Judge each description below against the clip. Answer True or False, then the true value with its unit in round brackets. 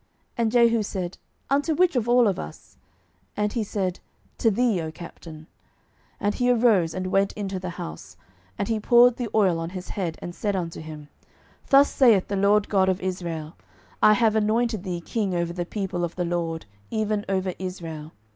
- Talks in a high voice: True (195 Hz)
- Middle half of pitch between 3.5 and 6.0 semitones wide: True (4.2 semitones)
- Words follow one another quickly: False (185 wpm)